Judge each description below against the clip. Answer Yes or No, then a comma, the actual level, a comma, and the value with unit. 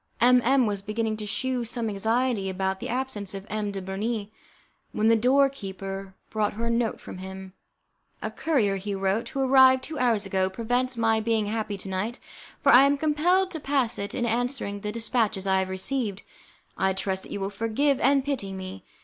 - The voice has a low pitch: No, high, 220 Hz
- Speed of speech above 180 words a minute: Yes, average, 200 wpm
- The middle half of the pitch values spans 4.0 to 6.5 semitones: Yes, average, 4.5 semitones